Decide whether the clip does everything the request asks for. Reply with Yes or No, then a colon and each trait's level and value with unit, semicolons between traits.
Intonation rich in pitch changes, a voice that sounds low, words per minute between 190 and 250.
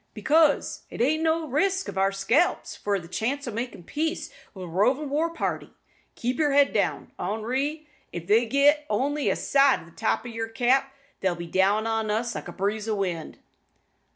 No: wide, 6.1 semitones; high, 240 Hz; average, 200 wpm